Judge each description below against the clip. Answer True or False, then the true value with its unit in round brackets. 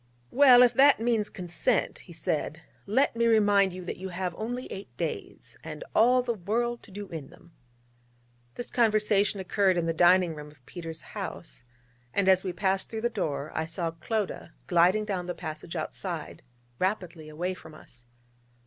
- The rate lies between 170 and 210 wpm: True (175 wpm)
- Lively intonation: False (4.4 semitones)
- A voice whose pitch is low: False (190 Hz)